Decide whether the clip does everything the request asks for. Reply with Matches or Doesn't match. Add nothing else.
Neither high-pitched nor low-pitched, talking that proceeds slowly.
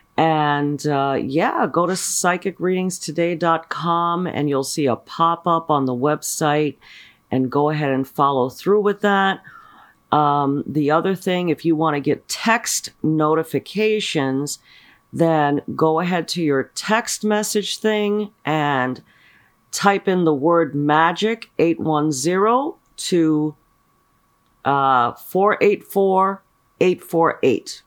Matches